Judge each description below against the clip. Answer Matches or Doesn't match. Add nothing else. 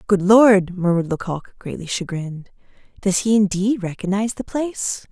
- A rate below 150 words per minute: Matches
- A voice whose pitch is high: Matches